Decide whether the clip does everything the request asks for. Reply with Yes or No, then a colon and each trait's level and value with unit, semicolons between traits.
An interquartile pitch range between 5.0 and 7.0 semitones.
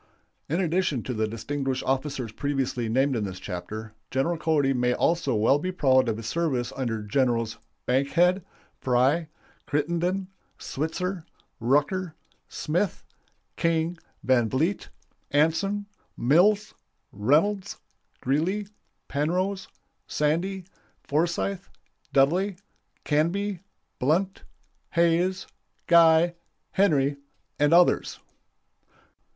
Yes: wide, 5.4 semitones